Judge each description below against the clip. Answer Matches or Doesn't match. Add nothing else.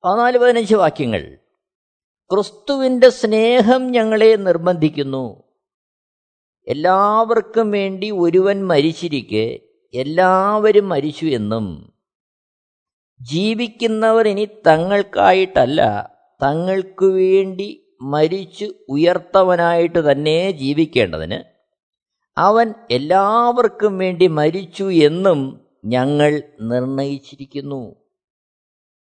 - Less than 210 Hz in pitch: Matches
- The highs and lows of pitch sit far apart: Matches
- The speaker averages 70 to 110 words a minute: Doesn't match